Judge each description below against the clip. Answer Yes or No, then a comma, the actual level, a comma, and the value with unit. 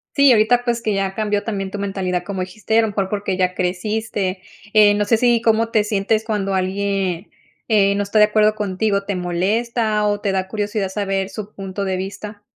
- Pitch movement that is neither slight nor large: No, narrow, 2.0 semitones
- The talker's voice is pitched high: Yes, high, 205 Hz